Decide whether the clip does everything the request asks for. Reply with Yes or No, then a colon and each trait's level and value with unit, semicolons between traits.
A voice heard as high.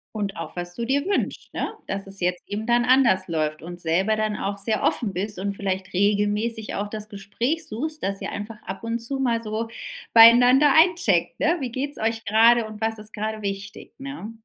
Yes: high, 215 Hz